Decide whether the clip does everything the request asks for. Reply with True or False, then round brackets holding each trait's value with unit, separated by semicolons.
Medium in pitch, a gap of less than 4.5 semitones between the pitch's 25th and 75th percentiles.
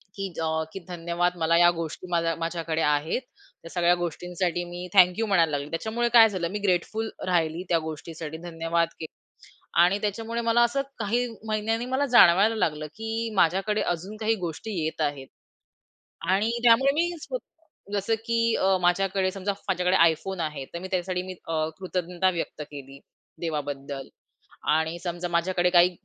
True (180 Hz; 4.1 semitones)